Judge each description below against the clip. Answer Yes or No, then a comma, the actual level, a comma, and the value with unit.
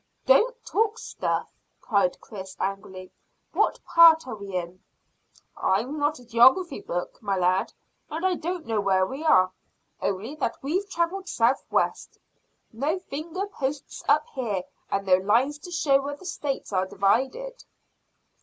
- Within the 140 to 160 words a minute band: Yes, average, 150 wpm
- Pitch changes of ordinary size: No, wide, 8.8 semitones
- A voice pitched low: No, very high, 265 Hz